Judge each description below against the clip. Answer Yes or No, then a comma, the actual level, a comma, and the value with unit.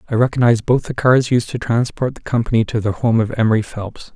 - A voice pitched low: Yes, low, 115 Hz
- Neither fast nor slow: No, fast, 230 wpm